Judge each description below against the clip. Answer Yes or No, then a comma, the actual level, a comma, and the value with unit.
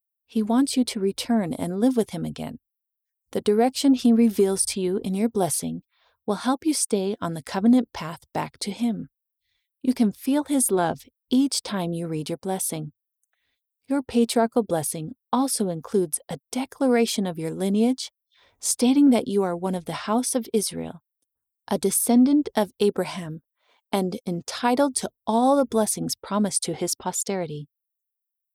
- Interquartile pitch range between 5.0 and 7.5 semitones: Yes, wide, 5.4 semitones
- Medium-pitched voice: No, high, 205 Hz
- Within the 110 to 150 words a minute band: No, average, 160 wpm